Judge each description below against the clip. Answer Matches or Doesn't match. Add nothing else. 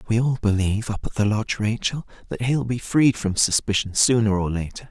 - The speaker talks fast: Matches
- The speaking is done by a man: Matches